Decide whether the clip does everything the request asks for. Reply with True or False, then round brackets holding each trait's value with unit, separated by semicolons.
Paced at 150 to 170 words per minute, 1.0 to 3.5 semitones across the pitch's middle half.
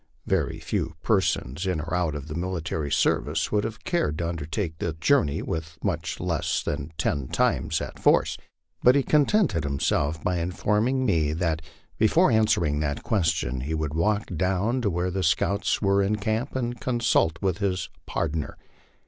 False (165 wpm; 5.3 semitones)